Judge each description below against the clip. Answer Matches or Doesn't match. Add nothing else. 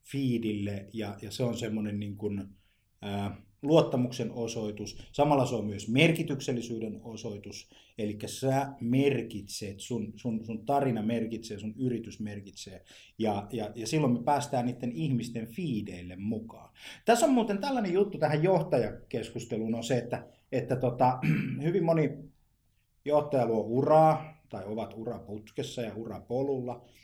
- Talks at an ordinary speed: Matches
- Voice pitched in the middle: Doesn't match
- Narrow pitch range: Doesn't match